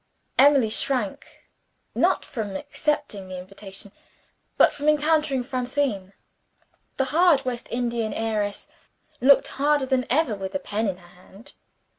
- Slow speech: Yes, slow, 130 wpm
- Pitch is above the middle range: Yes, high, 245 Hz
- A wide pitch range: Yes, wide, 5.9 semitones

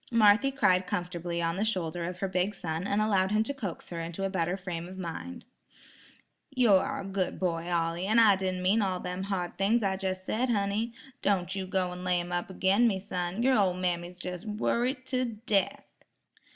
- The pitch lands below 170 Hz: No, high, 190 Hz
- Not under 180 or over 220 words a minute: Yes, fast, 205 wpm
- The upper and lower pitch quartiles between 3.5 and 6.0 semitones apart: No, average, 2.9 semitones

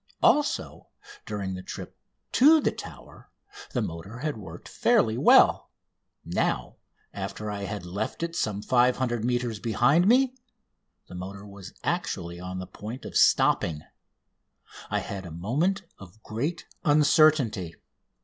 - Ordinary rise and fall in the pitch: No, wide, 7.4 semitones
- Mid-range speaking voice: No, low, 110 Hz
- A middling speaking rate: No, slow, 130 wpm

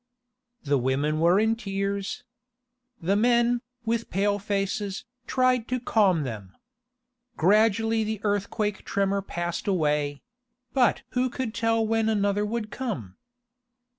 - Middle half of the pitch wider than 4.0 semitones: No, average, 3.6 semitones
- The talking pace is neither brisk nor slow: No, slow, 120 wpm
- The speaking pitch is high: Yes, high, 205 Hz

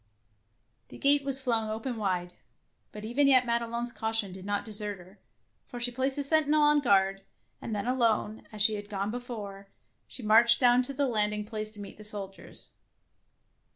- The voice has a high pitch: Yes, high, 220 Hz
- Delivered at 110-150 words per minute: No, average, 185 wpm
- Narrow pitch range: No, average, 3.4 semitones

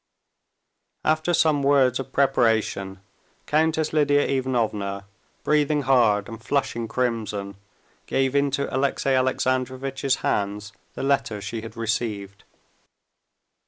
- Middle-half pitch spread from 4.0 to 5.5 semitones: Yes, average, 4.3 semitones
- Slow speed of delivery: Yes, slow, 100 wpm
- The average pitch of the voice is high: No, low, 130 Hz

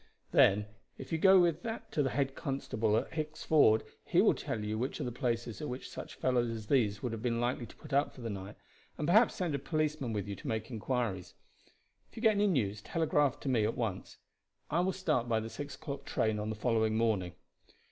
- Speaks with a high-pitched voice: No, low, 125 Hz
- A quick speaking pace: Yes, fast, 230 wpm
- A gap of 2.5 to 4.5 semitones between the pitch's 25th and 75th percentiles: No, wide, 5.5 semitones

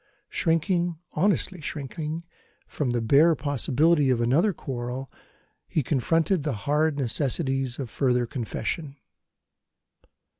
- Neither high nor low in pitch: Yes, medium, 145 Hz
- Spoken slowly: Yes, slow, 105 wpm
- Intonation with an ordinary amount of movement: Yes, average, 4.4 semitones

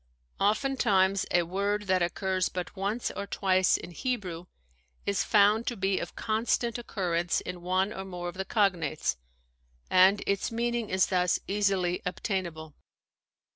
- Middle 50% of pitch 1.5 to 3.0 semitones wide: Yes, narrow, 2.5 semitones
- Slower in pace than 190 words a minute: Yes, average, 145 wpm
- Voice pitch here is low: No, high, 190 Hz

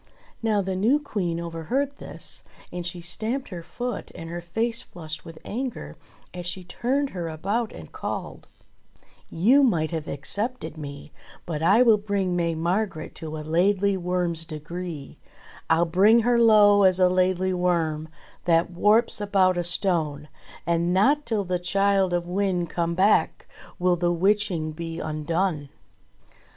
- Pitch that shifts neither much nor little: Yes, average, 3.7 semitones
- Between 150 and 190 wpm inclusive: Yes, average, 155 wpm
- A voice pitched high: No, medium, 180 Hz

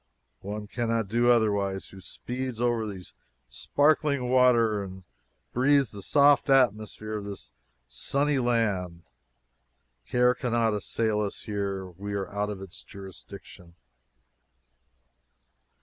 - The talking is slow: Yes, slow, 120 wpm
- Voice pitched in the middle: No, low, 110 Hz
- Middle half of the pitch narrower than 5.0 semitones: Yes, average, 3.8 semitones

